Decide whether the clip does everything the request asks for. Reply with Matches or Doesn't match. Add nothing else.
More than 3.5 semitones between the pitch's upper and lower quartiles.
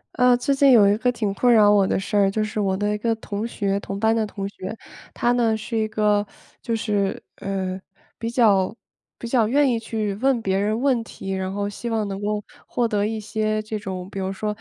Doesn't match